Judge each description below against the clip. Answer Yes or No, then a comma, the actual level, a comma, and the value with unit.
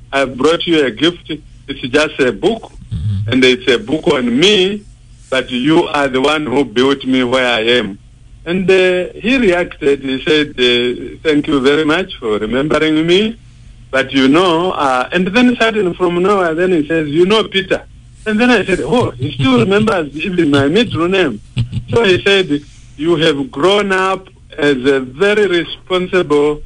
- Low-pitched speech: No, medium, 150 Hz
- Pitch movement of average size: No, wide, 6.0 semitones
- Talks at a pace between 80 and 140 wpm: No, average, 180 wpm